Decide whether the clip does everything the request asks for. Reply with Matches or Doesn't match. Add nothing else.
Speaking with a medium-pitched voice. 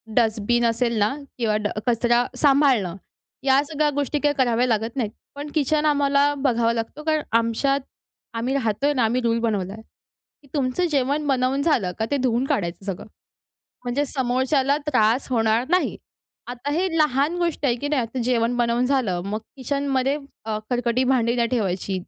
Doesn't match